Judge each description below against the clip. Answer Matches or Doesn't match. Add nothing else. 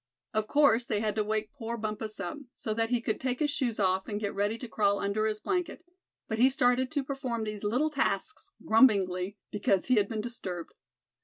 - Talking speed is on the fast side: Matches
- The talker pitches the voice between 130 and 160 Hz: Doesn't match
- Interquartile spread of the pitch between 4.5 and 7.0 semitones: Doesn't match